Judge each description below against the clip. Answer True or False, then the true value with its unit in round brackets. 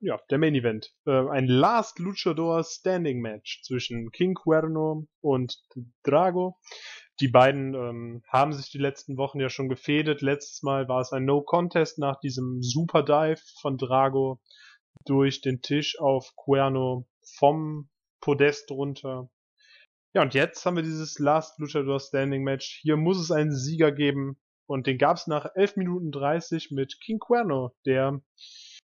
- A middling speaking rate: True (155 wpm)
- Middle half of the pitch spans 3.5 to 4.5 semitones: False (2.9 semitones)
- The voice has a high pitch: False (140 Hz)